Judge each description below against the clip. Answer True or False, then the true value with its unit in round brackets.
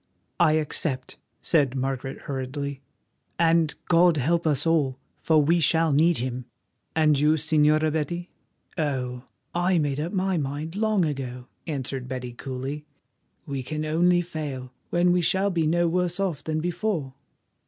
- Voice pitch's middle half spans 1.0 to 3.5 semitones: False (4.0 semitones)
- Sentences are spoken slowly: False (145 wpm)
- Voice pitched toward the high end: False (155 Hz)